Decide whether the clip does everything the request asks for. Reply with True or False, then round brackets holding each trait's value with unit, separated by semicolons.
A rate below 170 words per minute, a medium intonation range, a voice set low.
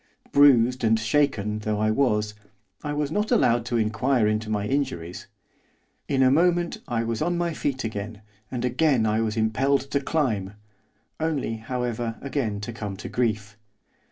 True (160 wpm; 4.4 semitones; 120 Hz)